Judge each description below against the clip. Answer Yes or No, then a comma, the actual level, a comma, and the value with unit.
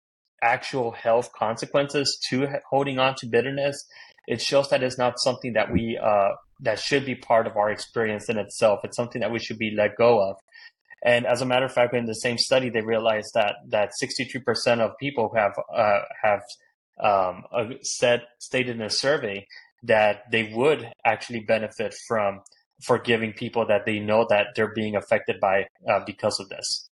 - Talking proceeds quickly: No, average, 180 wpm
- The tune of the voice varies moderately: Yes, average, 3.3 semitones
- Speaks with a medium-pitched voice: No, low, 120 Hz